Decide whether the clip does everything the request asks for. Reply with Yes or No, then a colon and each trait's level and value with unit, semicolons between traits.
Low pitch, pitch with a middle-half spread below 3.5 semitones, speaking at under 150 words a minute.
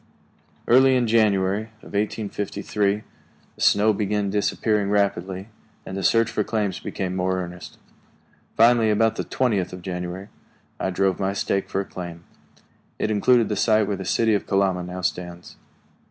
No: low, 100 Hz; narrow, 2.5 semitones; average, 155 wpm